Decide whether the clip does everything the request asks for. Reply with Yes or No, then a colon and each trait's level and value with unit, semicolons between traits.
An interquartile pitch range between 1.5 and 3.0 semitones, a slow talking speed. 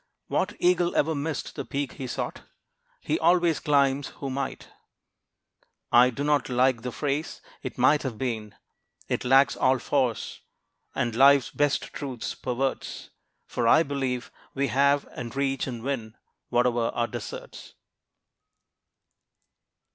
Yes: narrow, 2.5 semitones; slow, 130 wpm